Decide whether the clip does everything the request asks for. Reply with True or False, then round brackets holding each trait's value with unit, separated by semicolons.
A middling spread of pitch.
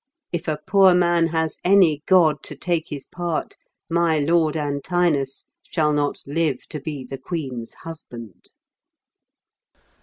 True (3.1 semitones)